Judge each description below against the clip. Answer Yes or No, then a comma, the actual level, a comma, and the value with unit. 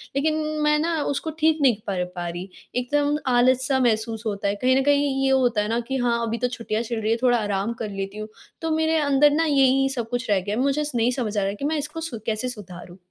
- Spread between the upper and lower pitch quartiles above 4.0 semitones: Yes, average, 4.9 semitones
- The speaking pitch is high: Yes, high, 245 Hz